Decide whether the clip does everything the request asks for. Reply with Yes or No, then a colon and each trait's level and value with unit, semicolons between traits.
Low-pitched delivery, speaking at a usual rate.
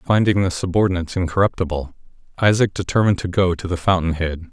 Yes: very low, 90 Hz; average, 160 wpm